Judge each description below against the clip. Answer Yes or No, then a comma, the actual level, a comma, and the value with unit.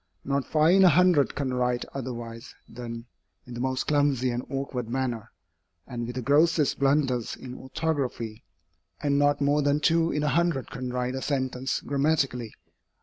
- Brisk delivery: No, average, 165 wpm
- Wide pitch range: No, average, 2.7 semitones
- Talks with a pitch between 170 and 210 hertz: No, low, 135 Hz